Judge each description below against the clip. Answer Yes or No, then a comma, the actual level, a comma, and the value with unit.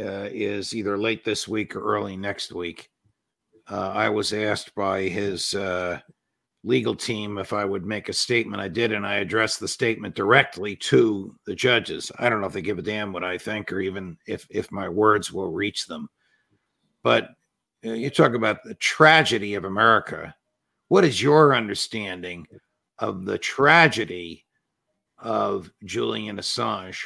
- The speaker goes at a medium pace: Yes, average, 165 wpm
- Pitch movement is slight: Yes, narrow, 2.3 semitones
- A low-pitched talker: Yes, low, 105 Hz